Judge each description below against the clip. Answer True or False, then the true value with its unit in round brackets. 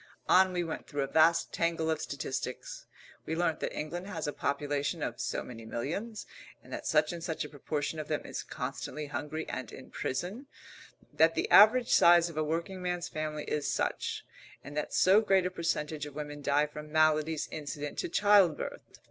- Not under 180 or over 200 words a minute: True (190 wpm)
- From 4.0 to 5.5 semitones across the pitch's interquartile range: False (3.0 semitones)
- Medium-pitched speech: True (155 Hz)